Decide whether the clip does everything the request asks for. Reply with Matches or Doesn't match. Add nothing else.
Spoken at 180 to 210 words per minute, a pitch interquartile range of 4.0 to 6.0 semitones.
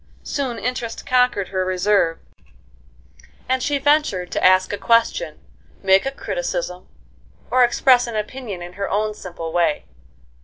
Doesn't match